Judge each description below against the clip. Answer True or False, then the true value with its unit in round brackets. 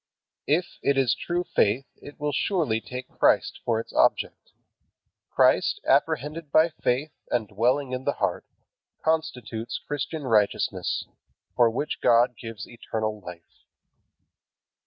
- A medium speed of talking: False (125 wpm)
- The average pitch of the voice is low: True (125 Hz)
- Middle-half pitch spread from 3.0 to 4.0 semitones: False (4.6 semitones)